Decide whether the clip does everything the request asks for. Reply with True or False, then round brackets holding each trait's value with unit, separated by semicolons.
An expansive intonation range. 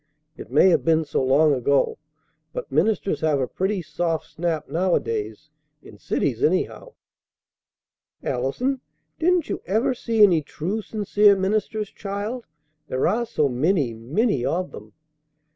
True (6.8 semitones)